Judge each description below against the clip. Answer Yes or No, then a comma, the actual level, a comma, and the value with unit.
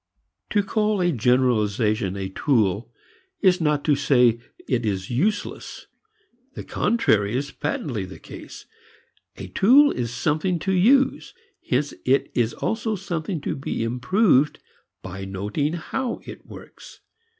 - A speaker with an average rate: No, slow, 130 wpm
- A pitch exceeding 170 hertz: No, medium, 140 Hz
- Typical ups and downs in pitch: No, wide, 8.5 semitones